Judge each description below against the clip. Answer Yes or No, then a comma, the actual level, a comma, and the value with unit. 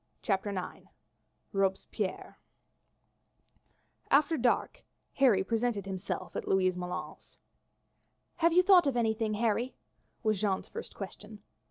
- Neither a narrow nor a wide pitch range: Yes, average, 4.2 semitones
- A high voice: Yes, high, 215 Hz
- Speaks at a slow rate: Yes, slow, 110 wpm